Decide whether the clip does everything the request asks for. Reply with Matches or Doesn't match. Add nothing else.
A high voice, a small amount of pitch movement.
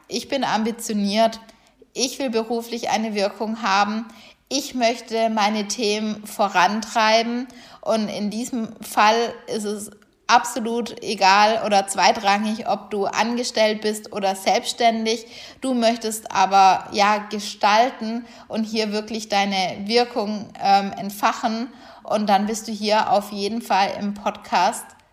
Matches